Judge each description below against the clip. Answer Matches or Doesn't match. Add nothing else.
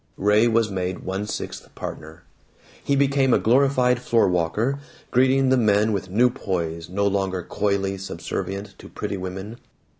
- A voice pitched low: Matches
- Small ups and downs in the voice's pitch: Doesn't match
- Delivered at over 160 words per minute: Doesn't match